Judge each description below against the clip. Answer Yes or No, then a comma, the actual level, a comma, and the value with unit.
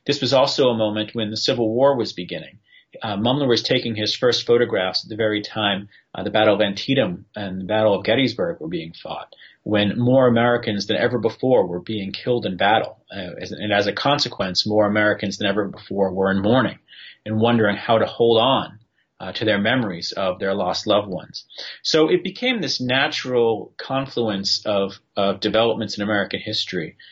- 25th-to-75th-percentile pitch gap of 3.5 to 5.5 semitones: No, average, 3.0 semitones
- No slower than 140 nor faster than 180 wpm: No, average, 190 wpm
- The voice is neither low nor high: No, low, 110 Hz